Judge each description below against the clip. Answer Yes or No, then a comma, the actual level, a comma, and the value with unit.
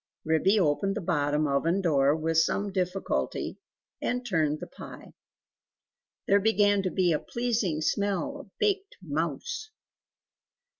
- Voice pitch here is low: No, medium, 185 Hz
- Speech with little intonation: No, average, 4.6 semitones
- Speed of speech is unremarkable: No, slow, 130 wpm